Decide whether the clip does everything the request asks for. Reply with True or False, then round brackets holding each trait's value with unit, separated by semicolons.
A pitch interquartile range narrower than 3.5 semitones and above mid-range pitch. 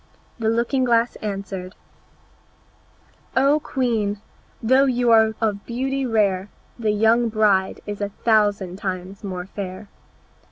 True (3.0 semitones; 215 Hz)